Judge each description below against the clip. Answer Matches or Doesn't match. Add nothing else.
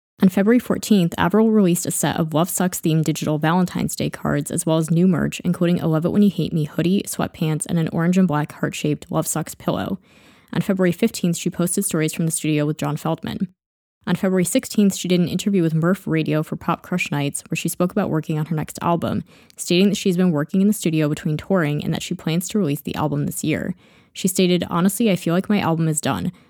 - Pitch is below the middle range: Doesn't match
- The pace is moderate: Doesn't match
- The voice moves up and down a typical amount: Matches